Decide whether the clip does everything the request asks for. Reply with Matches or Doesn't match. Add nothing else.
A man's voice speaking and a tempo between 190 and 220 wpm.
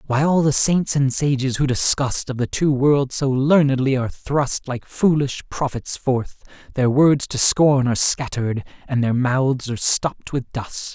Doesn't match